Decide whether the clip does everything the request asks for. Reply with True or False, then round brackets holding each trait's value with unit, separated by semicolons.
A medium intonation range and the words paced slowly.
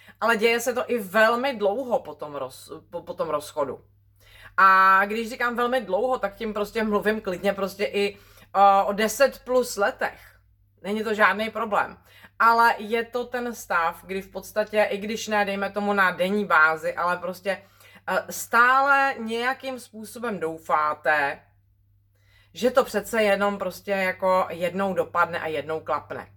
False (5.0 semitones; 155 wpm)